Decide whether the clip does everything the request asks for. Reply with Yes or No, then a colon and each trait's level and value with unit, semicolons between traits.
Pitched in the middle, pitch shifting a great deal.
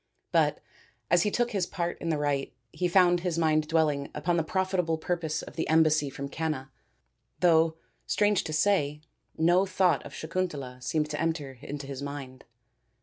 No: medium, 160 Hz; average, 3.4 semitones